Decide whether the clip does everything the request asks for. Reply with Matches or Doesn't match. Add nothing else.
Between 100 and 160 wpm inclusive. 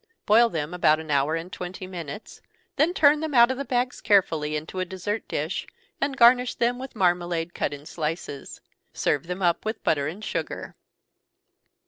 Doesn't match